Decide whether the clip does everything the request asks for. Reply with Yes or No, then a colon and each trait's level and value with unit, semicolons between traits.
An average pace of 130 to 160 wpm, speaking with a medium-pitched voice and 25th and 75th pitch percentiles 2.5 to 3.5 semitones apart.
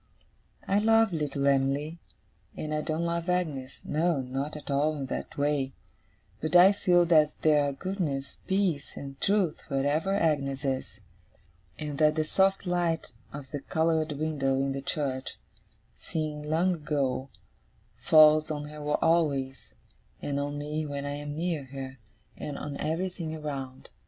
Yes: average, 150 wpm; medium, 150 Hz; average, 2.8 semitones